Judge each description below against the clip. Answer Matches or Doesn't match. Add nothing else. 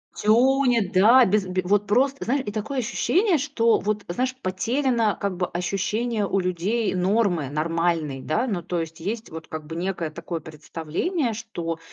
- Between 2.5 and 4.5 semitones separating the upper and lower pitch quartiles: Doesn't match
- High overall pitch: Matches